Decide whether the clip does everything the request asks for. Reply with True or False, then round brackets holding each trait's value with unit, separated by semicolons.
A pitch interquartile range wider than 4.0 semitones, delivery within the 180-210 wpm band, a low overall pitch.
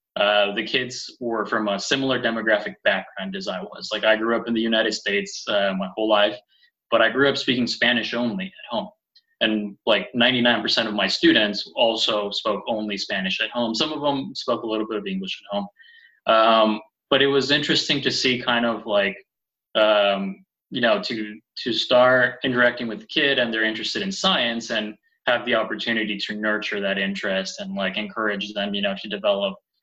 True (4.7 semitones; 195 wpm; 115 Hz)